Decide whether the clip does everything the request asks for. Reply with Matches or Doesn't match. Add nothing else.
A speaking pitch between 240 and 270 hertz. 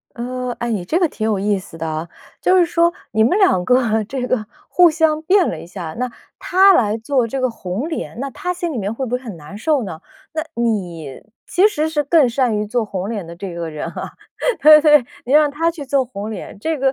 Matches